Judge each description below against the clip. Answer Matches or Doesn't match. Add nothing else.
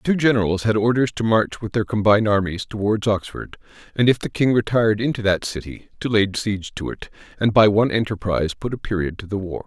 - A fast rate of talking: Matches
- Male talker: Matches